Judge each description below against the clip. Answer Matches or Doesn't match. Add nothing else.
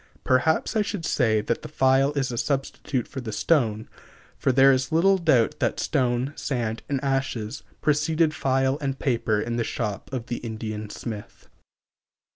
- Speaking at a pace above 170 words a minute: Doesn't match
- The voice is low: Matches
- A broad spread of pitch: Doesn't match